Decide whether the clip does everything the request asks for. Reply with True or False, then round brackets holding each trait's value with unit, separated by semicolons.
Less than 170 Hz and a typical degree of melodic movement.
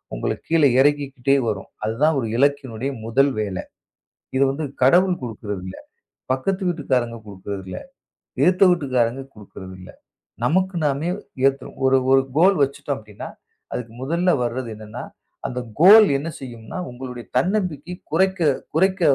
False (135 Hz; 6.1 semitones)